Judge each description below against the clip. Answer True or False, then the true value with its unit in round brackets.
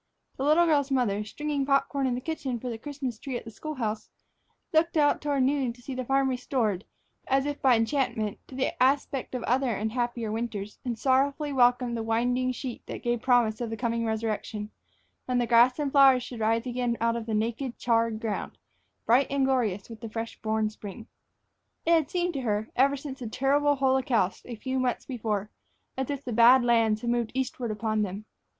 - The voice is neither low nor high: False (245 Hz)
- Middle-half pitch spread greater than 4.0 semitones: False (3.1 semitones)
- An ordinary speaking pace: False (210 wpm)